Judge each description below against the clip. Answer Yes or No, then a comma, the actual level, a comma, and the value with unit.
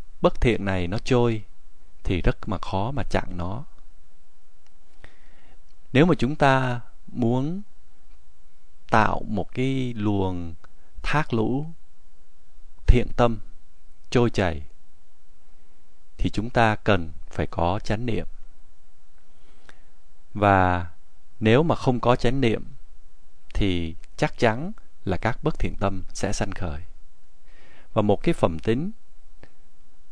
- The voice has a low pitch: Yes, low, 100 Hz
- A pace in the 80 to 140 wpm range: Yes, slow, 115 wpm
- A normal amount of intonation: No, wide, 6.4 semitones